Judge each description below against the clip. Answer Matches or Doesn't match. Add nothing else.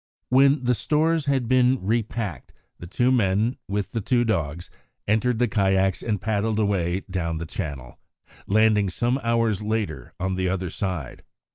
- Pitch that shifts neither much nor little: Matches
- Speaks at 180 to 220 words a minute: Doesn't match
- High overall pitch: Doesn't match